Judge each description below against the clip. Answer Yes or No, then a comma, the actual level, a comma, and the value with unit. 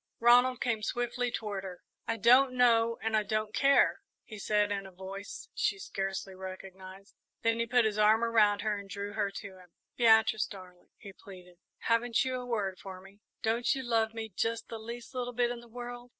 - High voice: Yes, high, 220 Hz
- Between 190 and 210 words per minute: Yes, average, 200 wpm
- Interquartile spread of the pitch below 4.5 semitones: Yes, average, 3.2 semitones